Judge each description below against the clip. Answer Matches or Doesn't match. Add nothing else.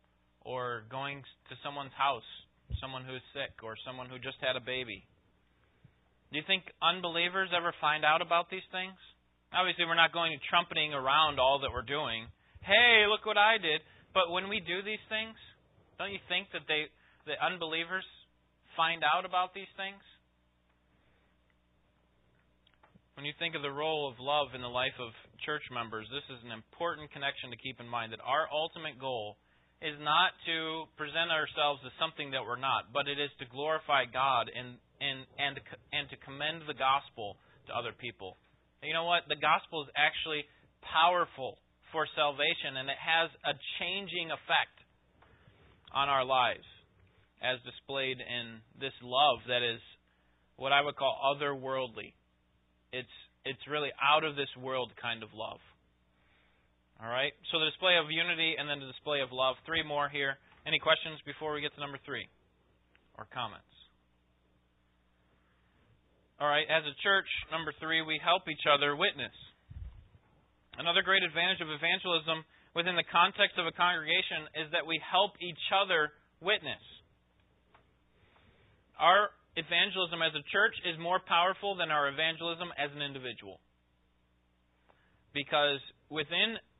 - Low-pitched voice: Doesn't match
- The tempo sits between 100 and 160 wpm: Matches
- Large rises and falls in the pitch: Matches